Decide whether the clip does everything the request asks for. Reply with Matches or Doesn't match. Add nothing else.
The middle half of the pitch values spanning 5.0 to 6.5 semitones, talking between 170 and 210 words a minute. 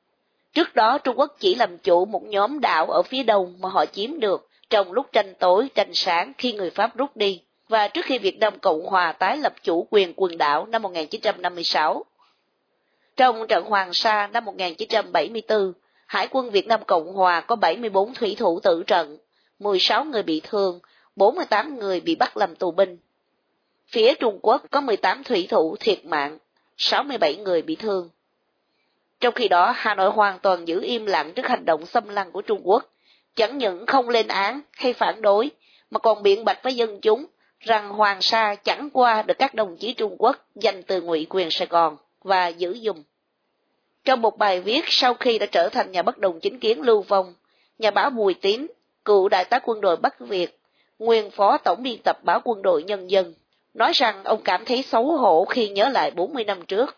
Doesn't match